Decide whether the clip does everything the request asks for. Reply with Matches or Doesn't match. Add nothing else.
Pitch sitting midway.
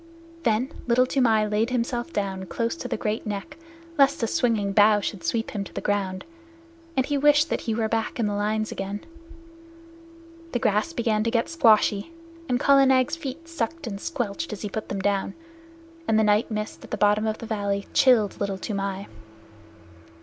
Doesn't match